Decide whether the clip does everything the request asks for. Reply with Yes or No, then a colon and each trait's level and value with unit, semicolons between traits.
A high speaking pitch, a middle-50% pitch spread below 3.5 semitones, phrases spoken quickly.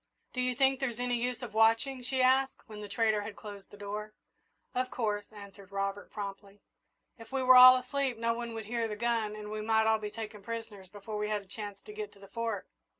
Yes: high, 220 Hz; average, 3.1 semitones; fast, 230 wpm